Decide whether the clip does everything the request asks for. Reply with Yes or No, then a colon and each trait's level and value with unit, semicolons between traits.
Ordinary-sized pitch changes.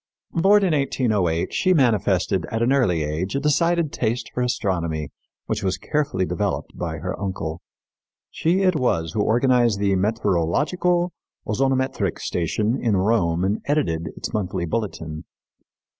No: wide, 7.4 semitones